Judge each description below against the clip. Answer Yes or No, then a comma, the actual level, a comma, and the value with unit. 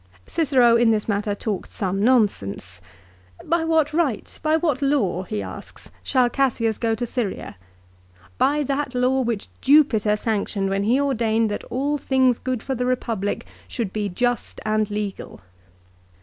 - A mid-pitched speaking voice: No, high, 235 Hz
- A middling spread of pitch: Yes, average, 4.4 semitones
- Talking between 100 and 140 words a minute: No, average, 160 wpm